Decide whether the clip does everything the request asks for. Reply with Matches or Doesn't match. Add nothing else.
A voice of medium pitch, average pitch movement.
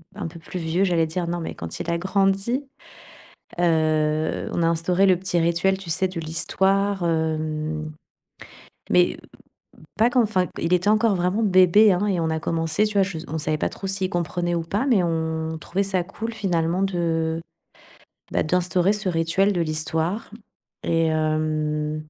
Matches